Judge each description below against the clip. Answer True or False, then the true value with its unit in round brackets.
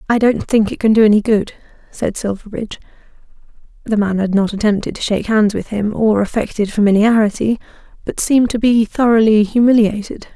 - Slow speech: False (170 wpm)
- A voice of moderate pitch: False (215 Hz)